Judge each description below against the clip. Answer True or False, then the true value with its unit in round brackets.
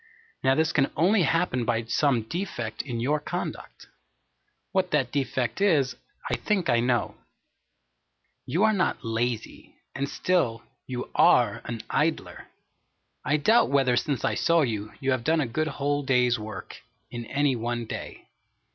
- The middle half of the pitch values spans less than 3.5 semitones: False (4.7 semitones)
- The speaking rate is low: False (155 wpm)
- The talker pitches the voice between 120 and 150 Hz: True (135 Hz)